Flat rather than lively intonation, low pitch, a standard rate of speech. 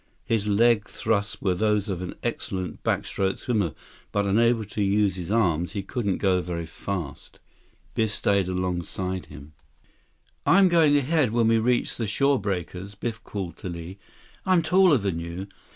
No: average, 3.8 semitones; low, 100 Hz; average, 165 wpm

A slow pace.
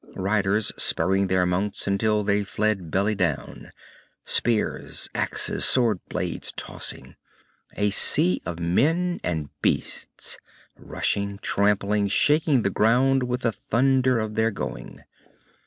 Yes: slow, 120 wpm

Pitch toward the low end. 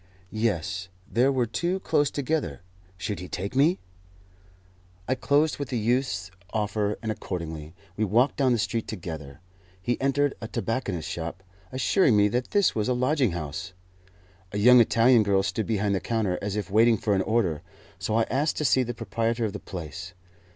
Yes: low, 110 Hz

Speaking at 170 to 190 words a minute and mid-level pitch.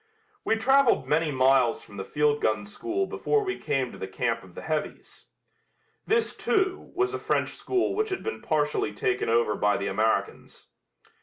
Yes: average, 175 wpm; medium, 150 Hz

